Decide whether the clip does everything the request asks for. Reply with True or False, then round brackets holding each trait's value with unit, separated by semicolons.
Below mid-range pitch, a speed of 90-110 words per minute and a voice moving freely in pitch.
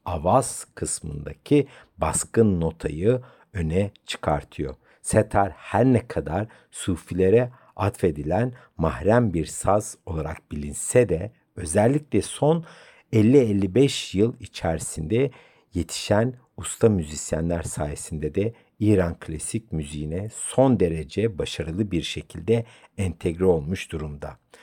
True (100 Hz; 95 wpm; 6.5 semitones)